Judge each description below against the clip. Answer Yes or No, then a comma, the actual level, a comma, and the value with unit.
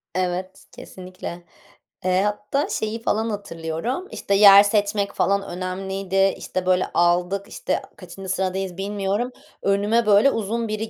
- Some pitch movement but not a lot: No, narrow, 2.2 semitones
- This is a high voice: Yes, high, 195 Hz